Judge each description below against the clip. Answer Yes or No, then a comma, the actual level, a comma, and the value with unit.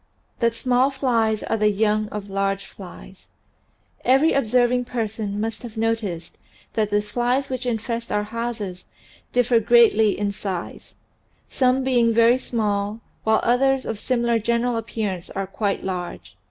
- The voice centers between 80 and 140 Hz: No, high, 225 Hz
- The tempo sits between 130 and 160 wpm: Yes, average, 150 wpm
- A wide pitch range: No, average, 2.8 semitones